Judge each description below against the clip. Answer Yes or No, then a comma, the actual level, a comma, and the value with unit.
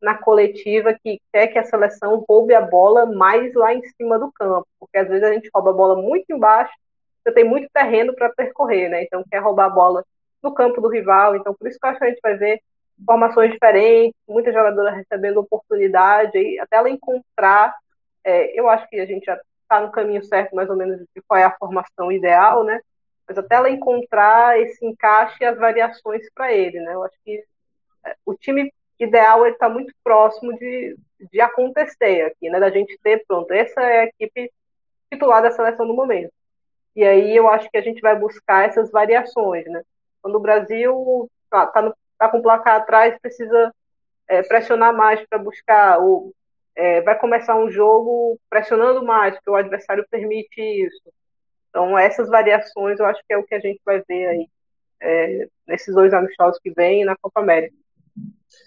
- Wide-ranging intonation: No, average, 2.9 semitones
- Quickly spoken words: Yes, fast, 195 wpm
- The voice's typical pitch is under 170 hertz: No, high, 220 Hz